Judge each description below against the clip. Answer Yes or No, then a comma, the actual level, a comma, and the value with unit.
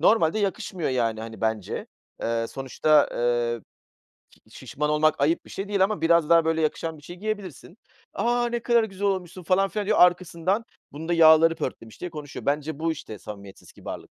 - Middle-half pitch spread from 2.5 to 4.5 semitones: No, average, 5.3 semitones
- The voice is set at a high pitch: No, medium, 165 Hz